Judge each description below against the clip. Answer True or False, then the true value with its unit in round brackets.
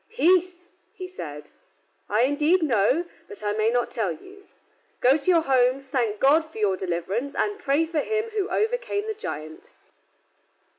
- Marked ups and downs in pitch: True (8.9 semitones)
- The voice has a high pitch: True (285 Hz)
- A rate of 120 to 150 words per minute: False (160 wpm)